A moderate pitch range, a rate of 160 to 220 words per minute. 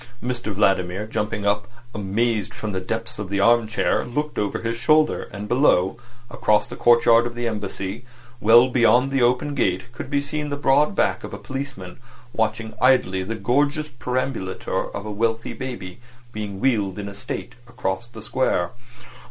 Yes: average, 3.9 semitones; average, 170 wpm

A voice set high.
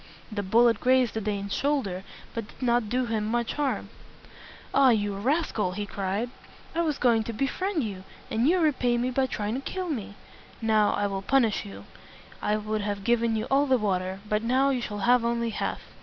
Yes: high, 230 Hz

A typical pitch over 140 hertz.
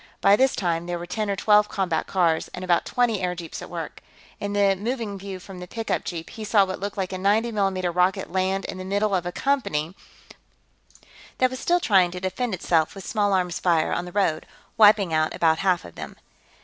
Yes: high, 190 Hz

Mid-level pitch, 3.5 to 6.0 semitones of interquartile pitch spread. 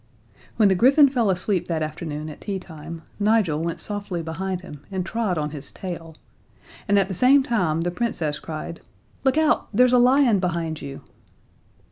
Yes: medium, 180 Hz; wide, 5.5 semitones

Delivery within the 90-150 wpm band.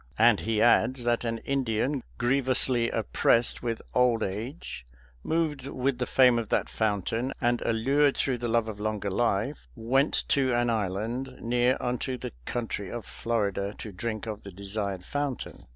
No: average, 160 wpm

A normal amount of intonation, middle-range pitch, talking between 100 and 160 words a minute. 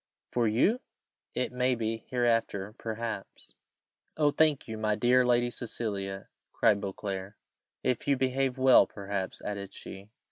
No: average, 3.8 semitones; low, 115 Hz; slow, 135 wpm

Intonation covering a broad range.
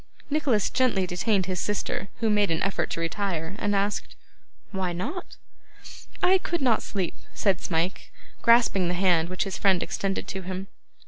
No: narrow, 2.6 semitones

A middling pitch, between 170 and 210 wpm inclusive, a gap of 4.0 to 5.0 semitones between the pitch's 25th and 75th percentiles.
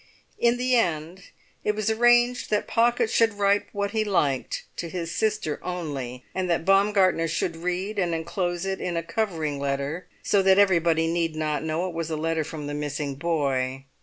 Yes: medium, 170 Hz; average, 185 wpm; average, 4.4 semitones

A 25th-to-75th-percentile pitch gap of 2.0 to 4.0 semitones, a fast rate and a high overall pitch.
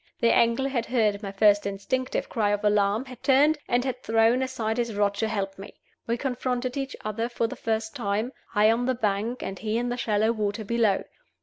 Yes: average, 3.0 semitones; fast, 210 wpm; high, 225 Hz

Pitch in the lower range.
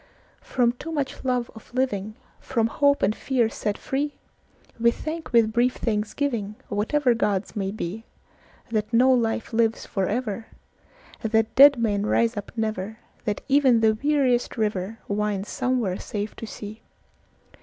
No: high, 225 Hz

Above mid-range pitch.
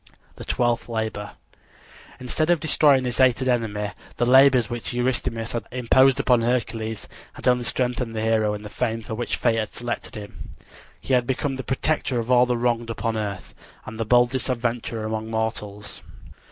No: low, 120 Hz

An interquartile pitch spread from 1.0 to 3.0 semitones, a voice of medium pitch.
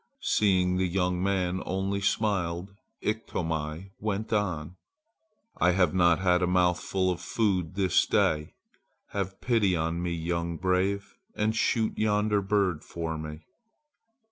No: narrow, 2.5 semitones; very low, 90 Hz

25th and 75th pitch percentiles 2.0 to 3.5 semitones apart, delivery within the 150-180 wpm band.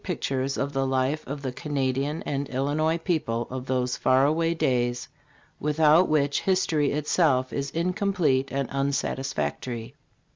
No: average, 3.0 semitones; average, 140 wpm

